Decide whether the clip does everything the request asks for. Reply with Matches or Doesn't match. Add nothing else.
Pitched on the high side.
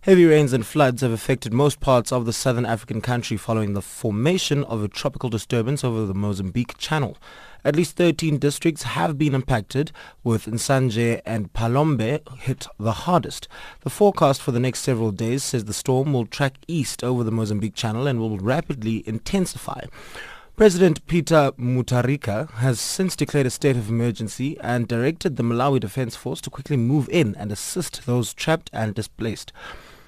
Doesn't match